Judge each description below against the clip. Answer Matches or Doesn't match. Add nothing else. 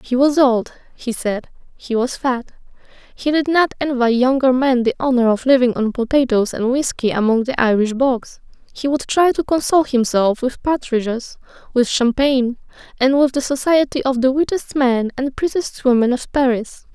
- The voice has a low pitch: Doesn't match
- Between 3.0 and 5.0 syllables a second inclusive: Matches